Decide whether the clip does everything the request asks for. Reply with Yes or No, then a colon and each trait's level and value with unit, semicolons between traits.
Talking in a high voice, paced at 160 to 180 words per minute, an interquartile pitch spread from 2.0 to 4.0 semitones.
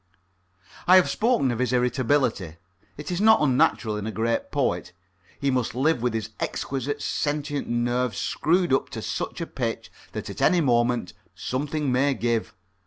No: low, 130 Hz; average, 165 wpm; average, 3.7 semitones